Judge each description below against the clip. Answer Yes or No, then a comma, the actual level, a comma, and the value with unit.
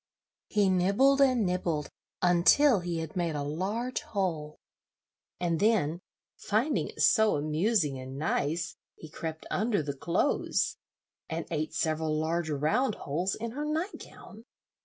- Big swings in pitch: Yes, wide, 5.8 semitones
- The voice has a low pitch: No, medium, 175 Hz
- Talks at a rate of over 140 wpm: No, slow, 135 wpm